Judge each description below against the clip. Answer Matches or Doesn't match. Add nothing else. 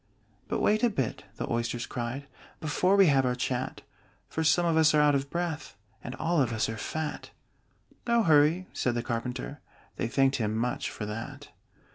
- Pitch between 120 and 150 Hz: Matches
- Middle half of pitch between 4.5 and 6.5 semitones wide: Matches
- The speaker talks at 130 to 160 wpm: Doesn't match